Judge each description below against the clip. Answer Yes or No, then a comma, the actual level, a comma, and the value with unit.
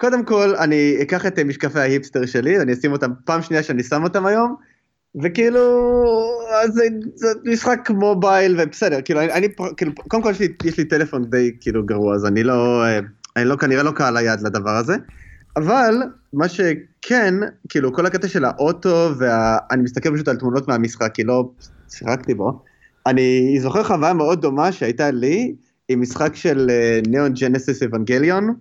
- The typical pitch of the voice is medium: Yes, medium, 150 Hz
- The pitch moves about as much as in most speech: No, wide, 7.7 semitones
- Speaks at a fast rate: Yes, fast, 165 wpm